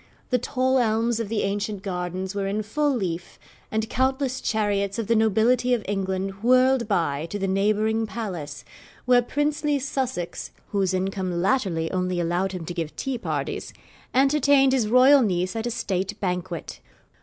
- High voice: Yes, high, 210 Hz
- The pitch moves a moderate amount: Yes, average, 5.0 semitones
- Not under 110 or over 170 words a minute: Yes, average, 160 wpm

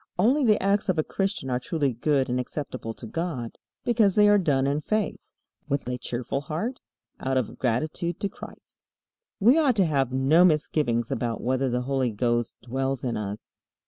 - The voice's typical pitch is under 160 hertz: Yes, medium, 140 Hz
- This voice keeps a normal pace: Yes, average, 180 wpm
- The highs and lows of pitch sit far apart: Yes, wide, 6.7 semitones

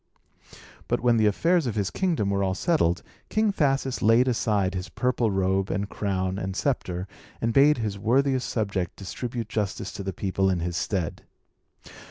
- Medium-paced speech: Yes, average, 170 wpm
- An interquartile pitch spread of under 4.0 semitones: No, average, 4.7 semitones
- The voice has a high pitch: No, low, 105 Hz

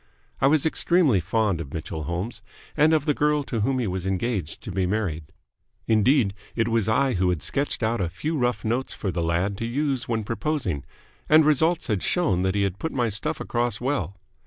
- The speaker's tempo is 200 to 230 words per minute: Yes, fast, 205 wpm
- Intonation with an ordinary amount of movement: No, wide, 6.6 semitones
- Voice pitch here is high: No, low, 115 Hz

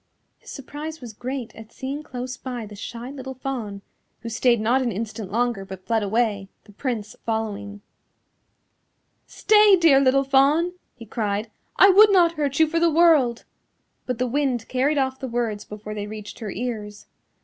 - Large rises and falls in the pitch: No, average, 4.3 semitones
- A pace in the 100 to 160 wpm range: No, average, 170 wpm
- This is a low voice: No, high, 245 Hz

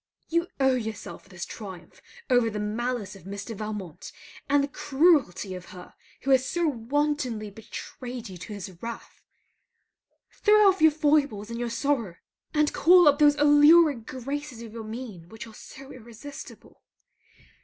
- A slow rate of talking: No, average, 155 wpm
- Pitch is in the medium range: No, high, 245 Hz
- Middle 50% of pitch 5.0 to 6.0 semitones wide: Yes, wide, 5.6 semitones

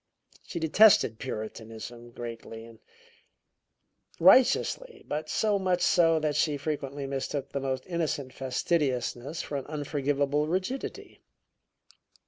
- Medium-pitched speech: Yes, medium, 145 Hz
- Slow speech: Yes, slow, 110 wpm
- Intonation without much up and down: No, average, 4.6 semitones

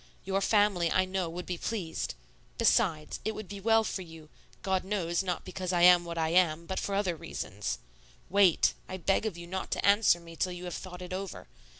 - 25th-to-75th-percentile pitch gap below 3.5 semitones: Yes, narrow, 2.4 semitones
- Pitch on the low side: No, medium, 185 Hz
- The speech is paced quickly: Yes, fast, 215 wpm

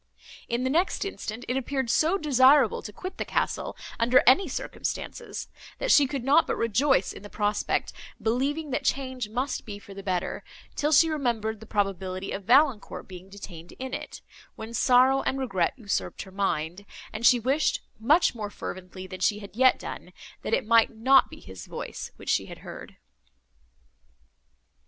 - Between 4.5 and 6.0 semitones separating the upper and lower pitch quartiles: Yes, average, 5.0 semitones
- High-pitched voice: Yes, high, 235 Hz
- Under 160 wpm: No, average, 175 wpm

